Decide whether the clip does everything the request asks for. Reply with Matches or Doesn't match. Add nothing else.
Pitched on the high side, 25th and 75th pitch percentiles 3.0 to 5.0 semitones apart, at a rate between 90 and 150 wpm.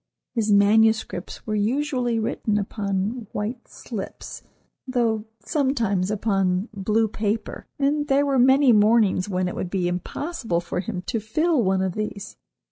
Matches